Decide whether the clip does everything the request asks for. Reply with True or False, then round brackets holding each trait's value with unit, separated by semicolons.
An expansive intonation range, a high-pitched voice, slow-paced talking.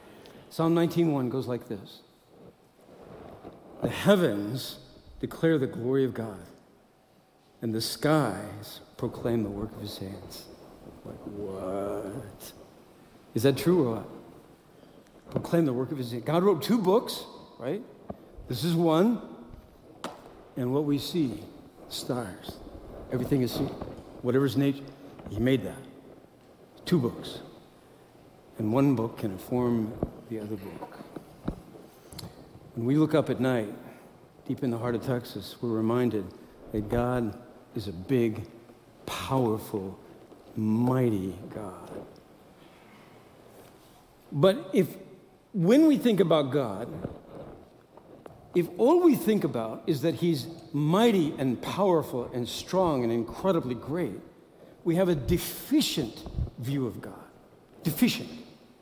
False (6.5 semitones; 130 Hz; 120 wpm)